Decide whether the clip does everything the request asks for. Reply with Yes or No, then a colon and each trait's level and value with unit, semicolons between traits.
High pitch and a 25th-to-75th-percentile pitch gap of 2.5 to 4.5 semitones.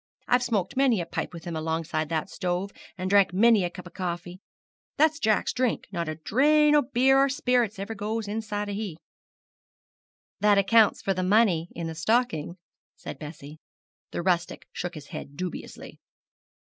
No: high, 195 Hz; average, 4.9 semitones